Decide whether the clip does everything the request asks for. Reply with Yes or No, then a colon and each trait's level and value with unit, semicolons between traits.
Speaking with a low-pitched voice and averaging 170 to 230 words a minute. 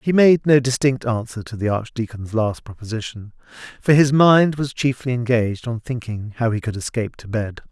Yes: low, 120 Hz; average, 185 wpm